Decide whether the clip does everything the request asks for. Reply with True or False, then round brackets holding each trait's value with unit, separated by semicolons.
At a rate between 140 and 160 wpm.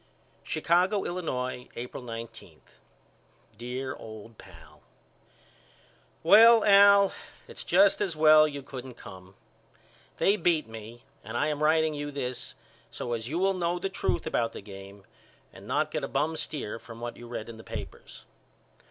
True (150 wpm)